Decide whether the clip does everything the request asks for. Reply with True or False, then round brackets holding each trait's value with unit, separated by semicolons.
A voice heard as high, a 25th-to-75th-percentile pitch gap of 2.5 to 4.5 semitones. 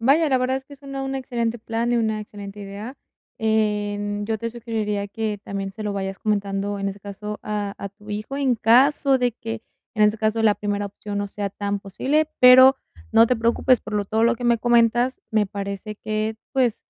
True (220 Hz; 2.8 semitones)